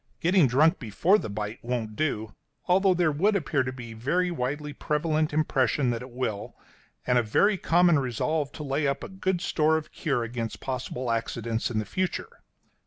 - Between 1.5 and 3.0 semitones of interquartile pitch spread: No, wide, 5.4 semitones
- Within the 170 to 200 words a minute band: Yes, average, 185 wpm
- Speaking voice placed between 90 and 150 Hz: Yes, medium, 140 Hz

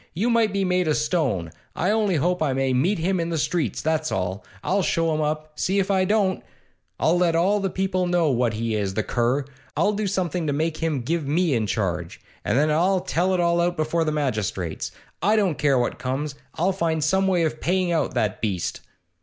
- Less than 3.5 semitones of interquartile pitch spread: No, wide, 5.4 semitones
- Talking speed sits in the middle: No, fast, 220 wpm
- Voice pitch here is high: No, medium, 160 Hz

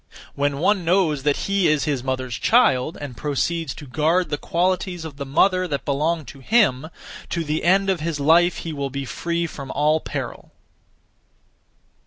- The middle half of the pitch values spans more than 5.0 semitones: No, average, 3.7 semitones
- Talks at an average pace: Yes, average, 175 wpm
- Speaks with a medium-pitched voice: Yes, medium, 155 Hz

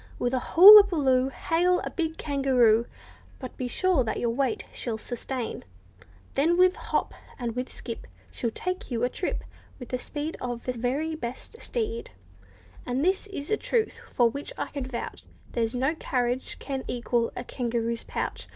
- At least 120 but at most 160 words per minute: No, average, 175 wpm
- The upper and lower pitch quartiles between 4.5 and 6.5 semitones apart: Yes, average, 5.2 semitones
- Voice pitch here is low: No, very high, 260 Hz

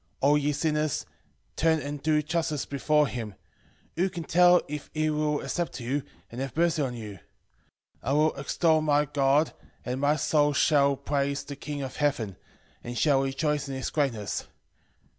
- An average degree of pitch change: No, narrow, 2.2 semitones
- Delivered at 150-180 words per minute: Yes, average, 170 wpm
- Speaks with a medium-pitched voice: Yes, medium, 145 Hz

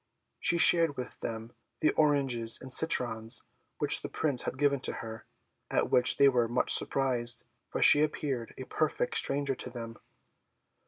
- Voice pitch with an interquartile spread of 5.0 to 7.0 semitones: No, average, 3.5 semitones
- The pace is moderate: Yes, average, 160 wpm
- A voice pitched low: Yes, low, 130 Hz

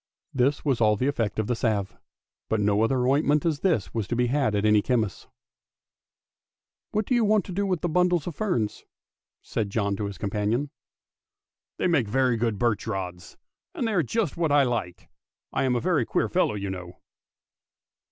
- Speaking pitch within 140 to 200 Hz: No, low, 120 Hz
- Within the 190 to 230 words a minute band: Yes, average, 195 wpm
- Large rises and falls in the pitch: Yes, wide, 6.2 semitones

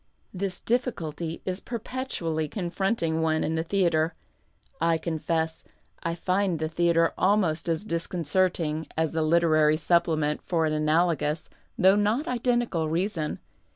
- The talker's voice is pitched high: No, medium, 170 Hz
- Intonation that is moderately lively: Yes, average, 3.1 semitones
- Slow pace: Yes, slow, 125 wpm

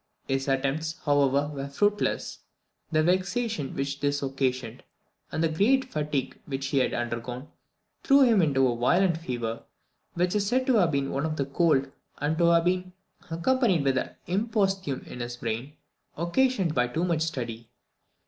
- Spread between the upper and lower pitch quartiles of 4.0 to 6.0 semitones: Yes, average, 5.3 semitones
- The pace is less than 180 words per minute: Yes, average, 160 wpm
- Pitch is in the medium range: Yes, medium, 150 Hz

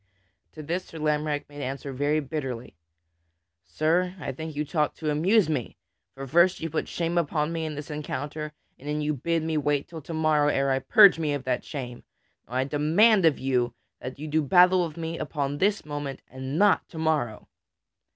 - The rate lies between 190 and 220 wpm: Yes, average, 195 wpm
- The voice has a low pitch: No, medium, 150 Hz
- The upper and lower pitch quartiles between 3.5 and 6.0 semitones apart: No, narrow, 2.6 semitones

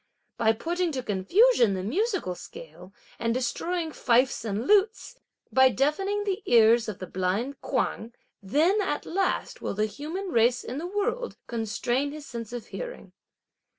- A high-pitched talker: Yes, very high, 260 Hz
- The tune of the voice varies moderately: No, wide, 8.7 semitones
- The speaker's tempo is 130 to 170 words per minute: Yes, average, 150 wpm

